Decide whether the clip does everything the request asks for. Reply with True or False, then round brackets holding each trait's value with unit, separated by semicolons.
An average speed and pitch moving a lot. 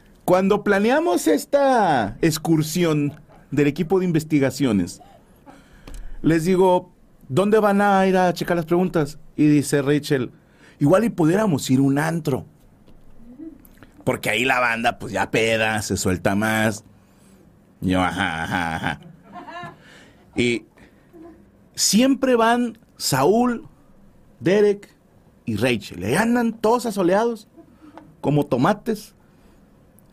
False (110 wpm; 8.3 semitones)